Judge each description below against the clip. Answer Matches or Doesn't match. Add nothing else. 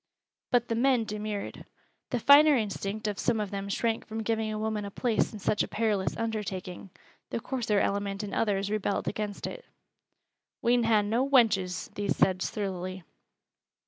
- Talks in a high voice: Matches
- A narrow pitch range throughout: Matches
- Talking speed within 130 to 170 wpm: Matches